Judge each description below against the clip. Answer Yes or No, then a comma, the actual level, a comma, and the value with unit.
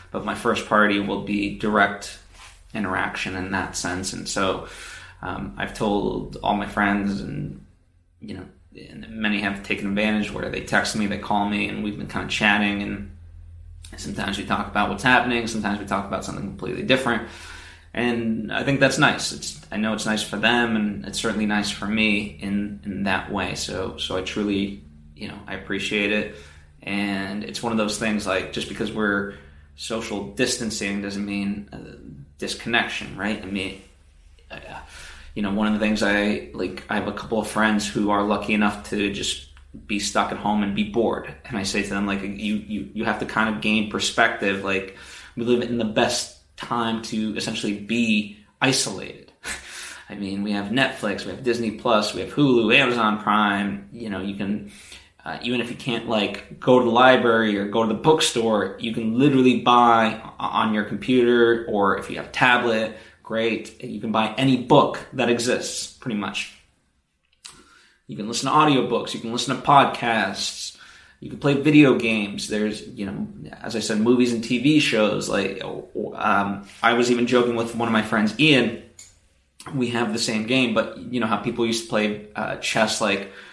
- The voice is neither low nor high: No, low, 105 Hz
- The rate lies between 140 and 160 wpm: No, average, 190 wpm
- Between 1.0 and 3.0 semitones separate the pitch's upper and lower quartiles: Yes, narrow, 2.5 semitones